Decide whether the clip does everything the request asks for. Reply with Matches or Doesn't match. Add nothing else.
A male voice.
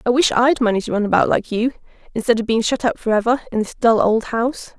Doesn't match